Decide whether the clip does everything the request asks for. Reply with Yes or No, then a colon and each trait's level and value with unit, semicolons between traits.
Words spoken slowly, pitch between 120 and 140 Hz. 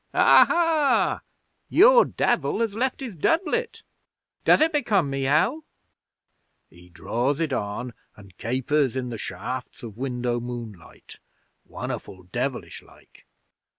Yes: slow, 120 wpm; low, 135 Hz